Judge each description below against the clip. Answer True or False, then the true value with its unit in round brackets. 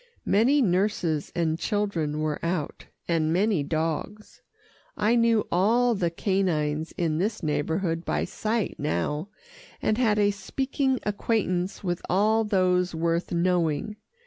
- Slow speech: True (125 wpm)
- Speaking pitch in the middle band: True (180 Hz)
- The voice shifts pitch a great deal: False (4.6 semitones)